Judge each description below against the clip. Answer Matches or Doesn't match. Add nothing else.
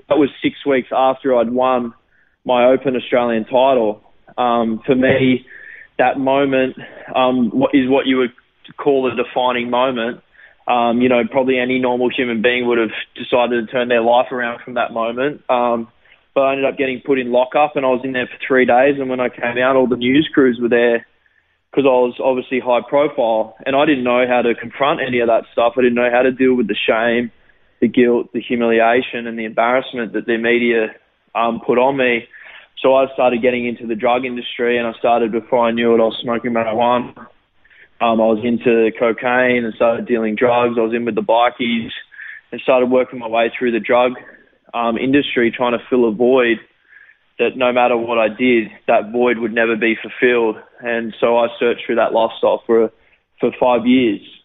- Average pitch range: Doesn't match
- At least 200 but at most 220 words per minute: Matches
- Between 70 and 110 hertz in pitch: Doesn't match